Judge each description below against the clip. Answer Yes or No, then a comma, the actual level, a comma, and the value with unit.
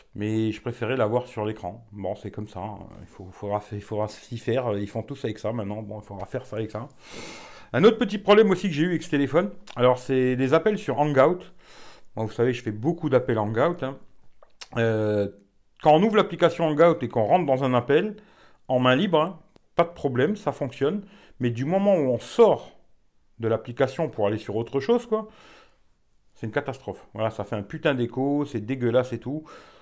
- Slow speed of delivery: No, average, 215 wpm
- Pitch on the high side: No, low, 125 Hz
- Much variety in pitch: Yes, wide, 6.5 semitones